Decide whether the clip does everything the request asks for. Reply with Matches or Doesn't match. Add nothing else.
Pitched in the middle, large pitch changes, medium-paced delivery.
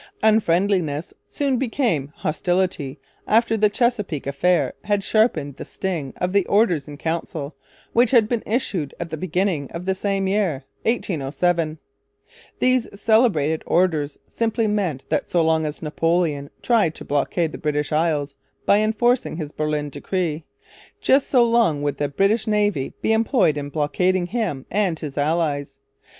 Matches